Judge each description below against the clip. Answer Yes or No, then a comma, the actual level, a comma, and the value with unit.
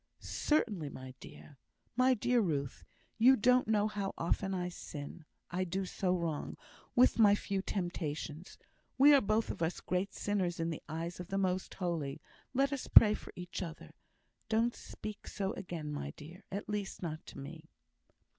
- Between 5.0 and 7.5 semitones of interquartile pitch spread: No, average, 4.3 semitones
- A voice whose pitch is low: No, medium, 185 Hz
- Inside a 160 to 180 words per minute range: Yes, average, 170 wpm